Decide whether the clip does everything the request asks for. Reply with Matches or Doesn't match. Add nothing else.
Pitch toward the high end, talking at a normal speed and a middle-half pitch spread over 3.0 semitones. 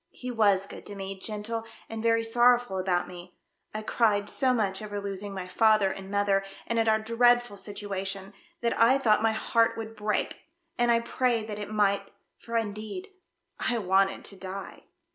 Doesn't match